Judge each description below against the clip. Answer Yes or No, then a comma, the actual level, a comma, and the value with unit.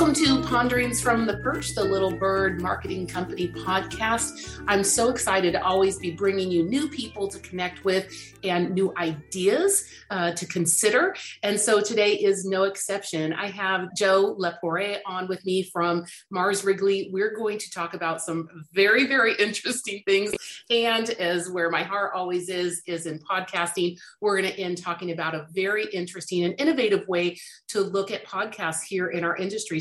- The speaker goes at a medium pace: Yes, average, 175 wpm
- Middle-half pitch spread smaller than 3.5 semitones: Yes, average, 2.7 semitones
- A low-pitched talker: No, high, 190 Hz